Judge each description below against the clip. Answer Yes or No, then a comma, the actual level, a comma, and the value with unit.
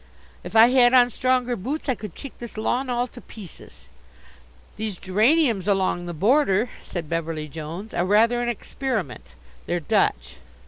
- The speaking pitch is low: No, high, 220 Hz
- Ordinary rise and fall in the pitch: No, wide, 5.8 semitones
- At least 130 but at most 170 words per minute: Yes, average, 155 wpm